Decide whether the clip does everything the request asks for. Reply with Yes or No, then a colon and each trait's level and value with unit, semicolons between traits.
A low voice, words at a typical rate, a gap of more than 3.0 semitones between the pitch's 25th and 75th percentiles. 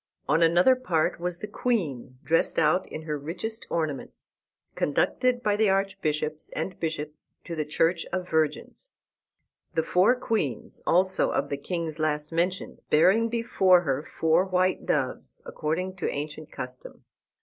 No: medium, 165 Hz; average, 145 wpm; average, 3.7 semitones